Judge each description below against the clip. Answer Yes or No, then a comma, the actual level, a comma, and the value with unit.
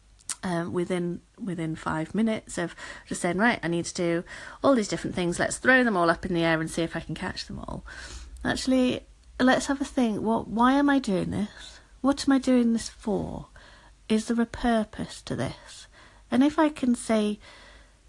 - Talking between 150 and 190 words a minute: No, average, 200 wpm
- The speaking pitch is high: Yes, high, 215 Hz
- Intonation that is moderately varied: No, wide, 6.8 semitones